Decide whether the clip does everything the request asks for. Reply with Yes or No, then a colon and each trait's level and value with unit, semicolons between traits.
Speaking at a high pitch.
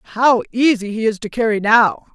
Yes: high, 225 Hz